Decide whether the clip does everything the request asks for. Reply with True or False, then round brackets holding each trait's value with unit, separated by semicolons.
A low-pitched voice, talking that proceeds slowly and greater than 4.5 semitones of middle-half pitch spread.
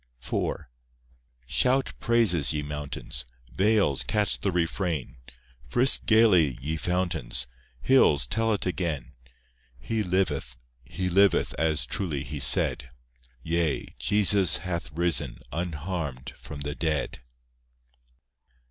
True (85 Hz; 105 wpm; 5.1 semitones)